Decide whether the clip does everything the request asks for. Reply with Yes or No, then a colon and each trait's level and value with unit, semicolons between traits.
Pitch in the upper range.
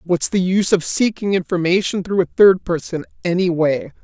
No: medium, 180 Hz